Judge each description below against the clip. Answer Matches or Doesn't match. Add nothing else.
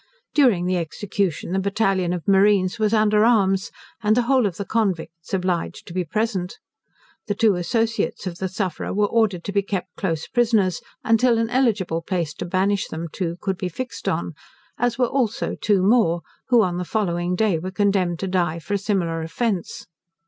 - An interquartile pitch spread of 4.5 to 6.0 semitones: Doesn't match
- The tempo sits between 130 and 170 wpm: Doesn't match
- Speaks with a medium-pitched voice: Doesn't match